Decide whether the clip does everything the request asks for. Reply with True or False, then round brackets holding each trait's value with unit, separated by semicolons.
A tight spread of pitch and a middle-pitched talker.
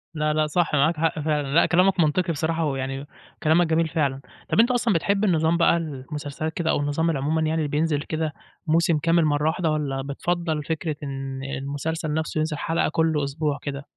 True (2.2 semitones; 155 Hz)